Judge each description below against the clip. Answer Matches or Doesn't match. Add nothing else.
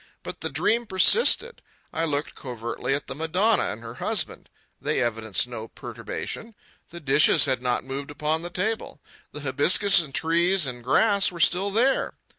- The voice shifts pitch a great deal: Matches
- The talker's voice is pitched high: Doesn't match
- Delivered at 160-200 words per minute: Matches